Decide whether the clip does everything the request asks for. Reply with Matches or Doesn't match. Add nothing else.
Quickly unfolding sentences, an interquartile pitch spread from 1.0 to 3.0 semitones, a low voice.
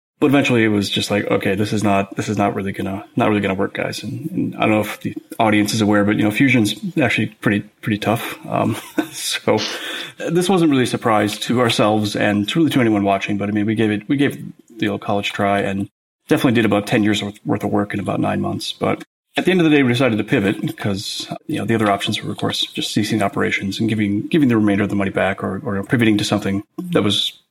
Matches